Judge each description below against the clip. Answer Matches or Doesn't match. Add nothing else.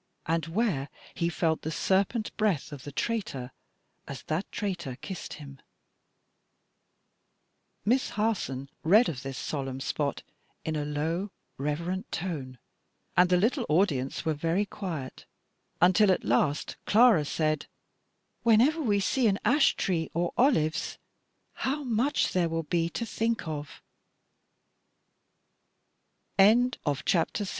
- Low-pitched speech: Doesn't match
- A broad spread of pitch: Matches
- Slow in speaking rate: Matches